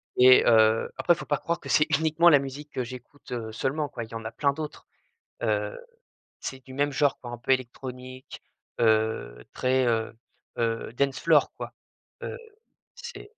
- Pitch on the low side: Yes, low, 130 Hz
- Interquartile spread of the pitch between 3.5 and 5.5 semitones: Yes, average, 4.0 semitones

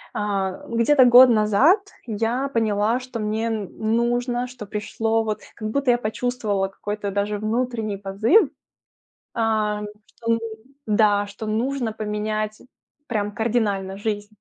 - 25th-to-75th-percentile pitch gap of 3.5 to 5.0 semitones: No, narrow, 2.4 semitones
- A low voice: No, high, 220 Hz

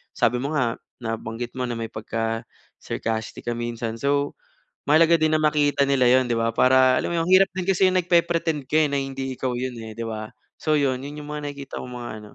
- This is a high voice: No, low, 130 Hz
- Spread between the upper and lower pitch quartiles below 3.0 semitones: No, average, 4.1 semitones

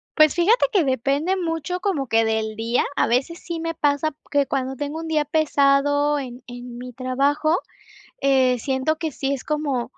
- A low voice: No, very high, 280 Hz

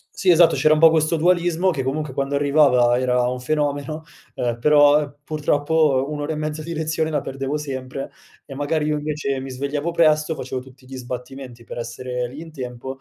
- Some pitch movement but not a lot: Yes, average, 3.0 semitones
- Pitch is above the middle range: No, medium, 145 Hz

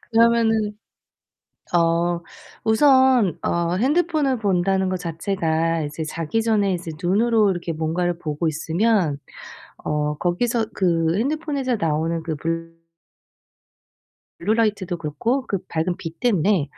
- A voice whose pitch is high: No, medium, 180 Hz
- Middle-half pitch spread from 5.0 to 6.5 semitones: Yes, average, 5.3 semitones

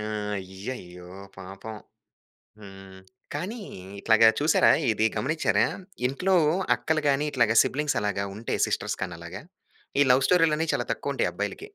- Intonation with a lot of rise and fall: Yes, wide, 7.6 semitones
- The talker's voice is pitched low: Yes, low, 115 Hz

